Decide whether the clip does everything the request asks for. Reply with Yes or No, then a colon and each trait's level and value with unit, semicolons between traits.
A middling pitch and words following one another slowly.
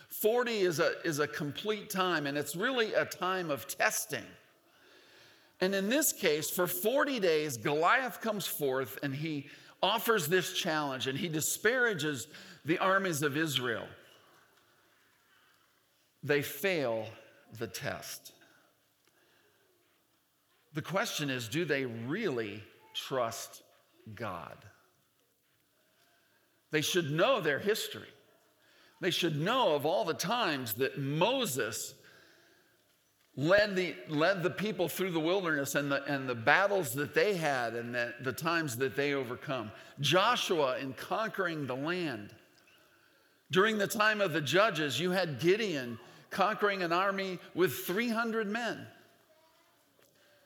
Yes: medium, 170 Hz; slow, 125 wpm